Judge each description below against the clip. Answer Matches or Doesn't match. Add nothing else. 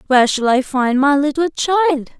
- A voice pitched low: Doesn't match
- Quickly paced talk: Doesn't match